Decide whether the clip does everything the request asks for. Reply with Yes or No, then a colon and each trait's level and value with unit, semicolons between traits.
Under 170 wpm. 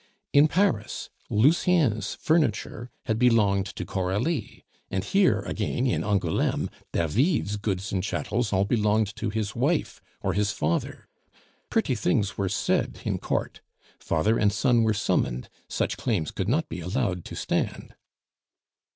Yes: average, 140 wpm